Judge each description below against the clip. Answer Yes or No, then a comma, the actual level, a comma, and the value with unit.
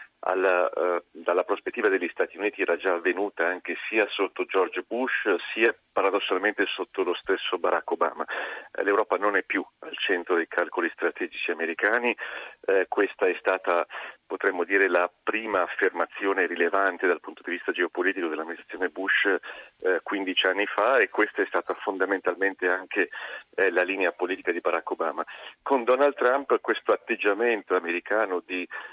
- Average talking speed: Yes, average, 155 wpm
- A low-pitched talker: Yes, low, 130 Hz